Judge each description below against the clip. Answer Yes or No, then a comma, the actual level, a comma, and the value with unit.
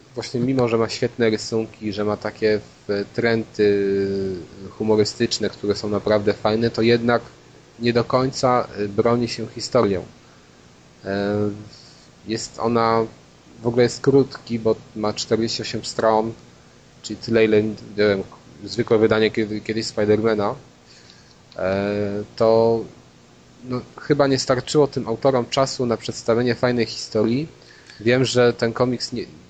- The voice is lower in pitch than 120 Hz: Yes, low, 110 Hz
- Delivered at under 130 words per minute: Yes, average, 115 wpm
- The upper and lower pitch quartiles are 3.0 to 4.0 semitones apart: No, narrow, 2.6 semitones